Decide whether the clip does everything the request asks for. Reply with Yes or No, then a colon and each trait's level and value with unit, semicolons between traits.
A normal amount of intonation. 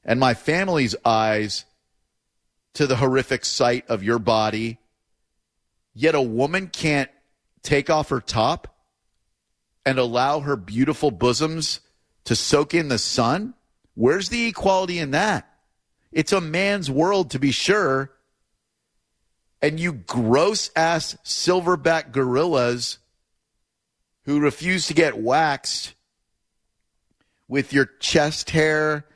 No: wide, 5.9 semitones